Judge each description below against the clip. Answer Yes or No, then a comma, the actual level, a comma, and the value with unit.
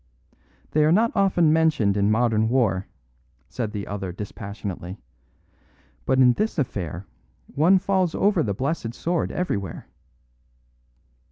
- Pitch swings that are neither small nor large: No, wide, 8.6 semitones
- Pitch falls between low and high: No, low, 120 Hz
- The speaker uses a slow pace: Yes, slow, 120 wpm